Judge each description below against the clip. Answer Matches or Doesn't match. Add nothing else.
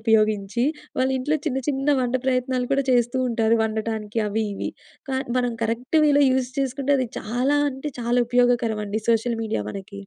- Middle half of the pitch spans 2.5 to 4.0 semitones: Matches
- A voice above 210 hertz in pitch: Matches